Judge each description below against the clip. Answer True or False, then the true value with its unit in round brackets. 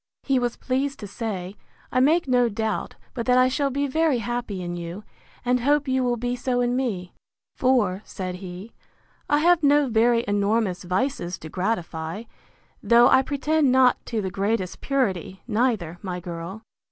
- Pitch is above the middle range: True (235 Hz)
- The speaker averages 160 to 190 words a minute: True (170 wpm)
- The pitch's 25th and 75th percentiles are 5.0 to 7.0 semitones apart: True (5.5 semitones)